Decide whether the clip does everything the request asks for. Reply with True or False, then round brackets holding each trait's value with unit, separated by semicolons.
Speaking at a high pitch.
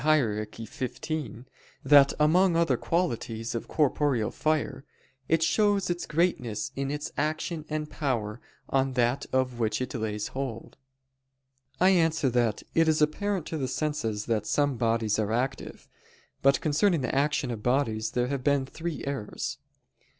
False (135 Hz)